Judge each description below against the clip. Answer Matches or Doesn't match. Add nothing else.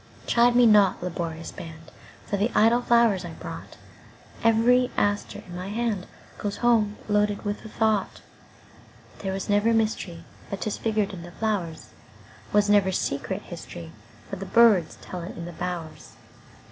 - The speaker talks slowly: Matches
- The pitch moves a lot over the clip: Doesn't match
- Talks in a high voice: Matches